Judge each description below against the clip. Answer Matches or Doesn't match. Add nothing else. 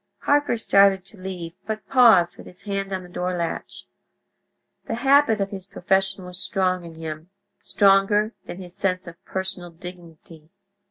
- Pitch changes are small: Matches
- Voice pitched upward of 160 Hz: Matches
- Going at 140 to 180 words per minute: Matches